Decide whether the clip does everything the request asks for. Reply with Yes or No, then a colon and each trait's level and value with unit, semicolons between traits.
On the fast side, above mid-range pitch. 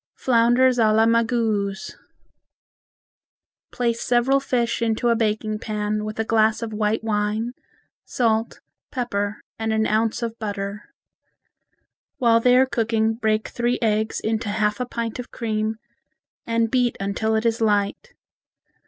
No: slow, 135 wpm; high, 225 Hz